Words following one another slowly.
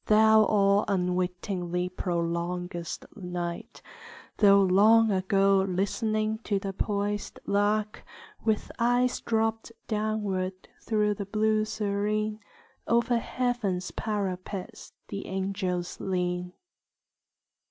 Yes: slow, 90 wpm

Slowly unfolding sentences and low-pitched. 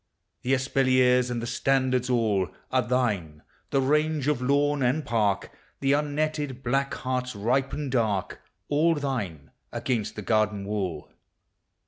Yes: slow, 130 wpm; low, 125 Hz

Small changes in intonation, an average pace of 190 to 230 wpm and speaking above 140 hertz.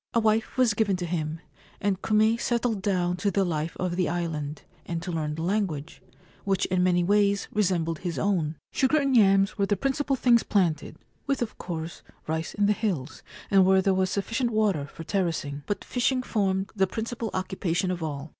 No: average, 4.1 semitones; average, 200 wpm; high, 190 Hz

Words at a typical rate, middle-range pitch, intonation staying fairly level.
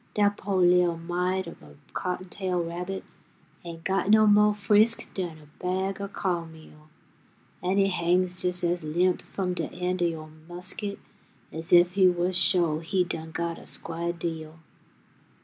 Yes: average, 165 wpm; medium, 180 Hz; narrow, 2.1 semitones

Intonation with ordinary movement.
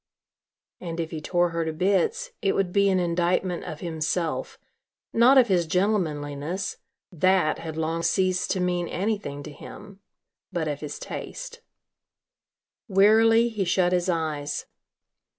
Yes: average, 3.6 semitones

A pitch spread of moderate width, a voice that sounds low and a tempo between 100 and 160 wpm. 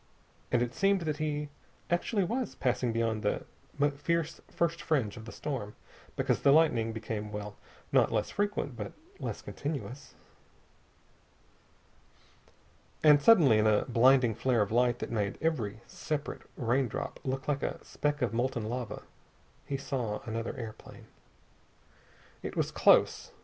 Yes: average, 4.8 semitones; low, 125 Hz; average, 140 wpm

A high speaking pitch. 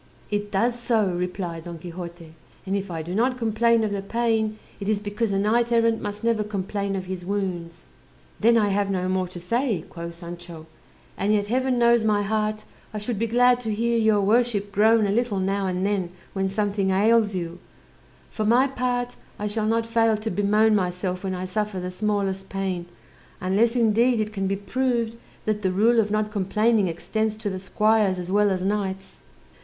Yes: high, 205 Hz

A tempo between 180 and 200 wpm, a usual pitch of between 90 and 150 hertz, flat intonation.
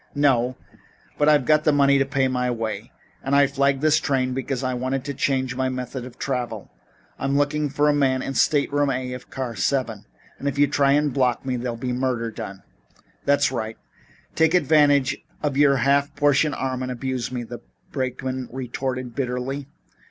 Yes: average, 185 wpm; low, 135 Hz; narrow, 2.0 semitones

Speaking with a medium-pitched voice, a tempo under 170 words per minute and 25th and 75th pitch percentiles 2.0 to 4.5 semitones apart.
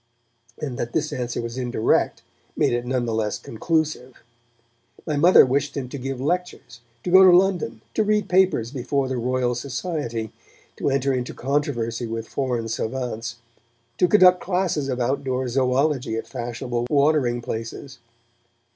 No: low, 130 Hz; average, 150 wpm; average, 3.8 semitones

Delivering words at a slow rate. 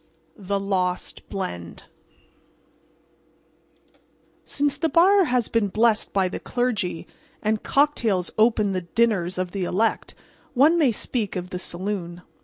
Yes: slow, 125 wpm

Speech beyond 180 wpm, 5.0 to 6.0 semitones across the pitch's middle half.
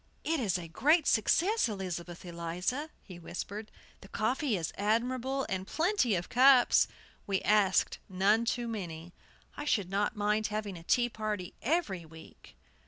No: average, 145 wpm; wide, 5.4 semitones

